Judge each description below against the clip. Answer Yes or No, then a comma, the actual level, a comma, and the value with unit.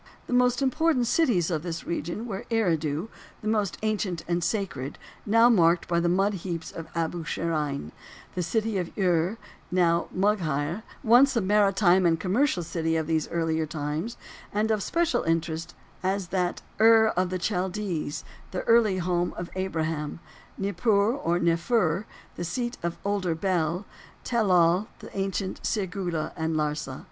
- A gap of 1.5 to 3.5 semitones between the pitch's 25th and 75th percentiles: No, average, 4.1 semitones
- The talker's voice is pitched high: No, medium, 180 Hz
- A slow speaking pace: No, average, 155 wpm